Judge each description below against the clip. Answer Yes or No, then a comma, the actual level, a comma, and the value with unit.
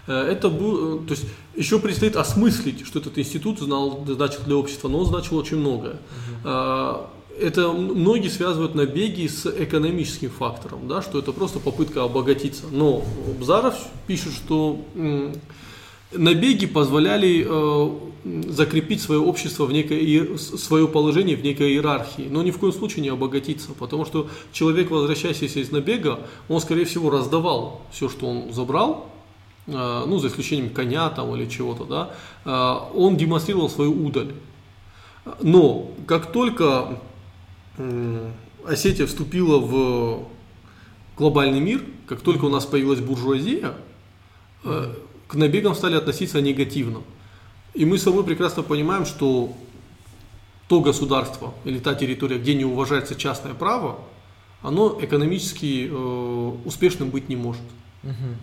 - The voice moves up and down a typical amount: Yes, average, 4.2 semitones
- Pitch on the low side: No, medium, 145 Hz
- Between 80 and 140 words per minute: Yes, average, 125 wpm